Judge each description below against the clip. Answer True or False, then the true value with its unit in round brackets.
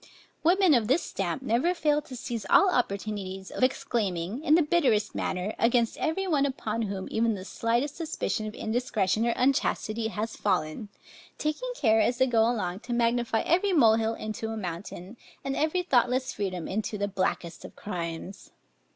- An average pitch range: True (5.0 semitones)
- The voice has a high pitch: True (230 Hz)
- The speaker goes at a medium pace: True (170 wpm)